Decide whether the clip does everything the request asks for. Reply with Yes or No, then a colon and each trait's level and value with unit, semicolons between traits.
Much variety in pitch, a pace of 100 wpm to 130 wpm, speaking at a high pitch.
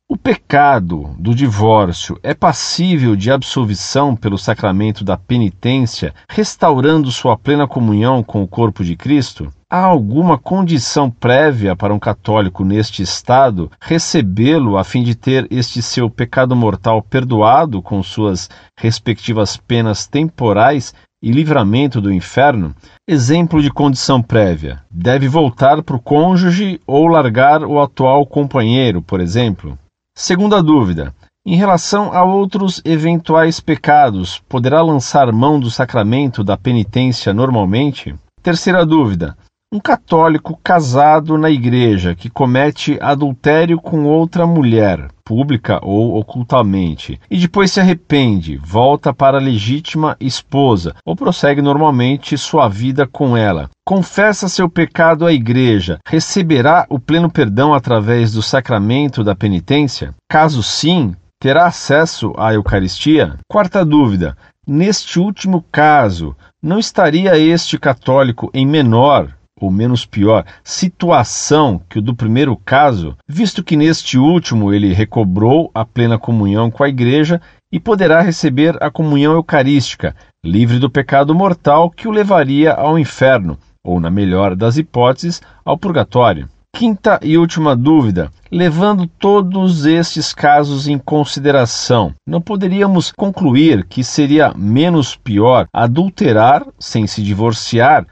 No: wide, 6.7 semitones; average, 125 wpm; low, 135 Hz